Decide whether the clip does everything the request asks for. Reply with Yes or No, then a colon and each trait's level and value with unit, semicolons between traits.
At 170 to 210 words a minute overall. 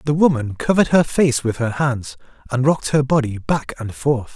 Yes: fast, 205 wpm